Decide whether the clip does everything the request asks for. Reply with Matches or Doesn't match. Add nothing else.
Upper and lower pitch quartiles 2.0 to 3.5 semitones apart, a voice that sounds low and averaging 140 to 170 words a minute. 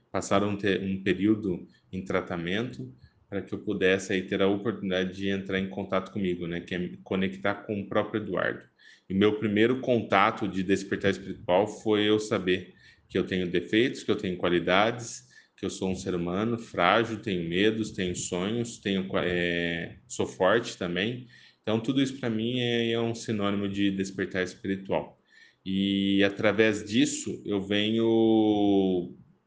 Matches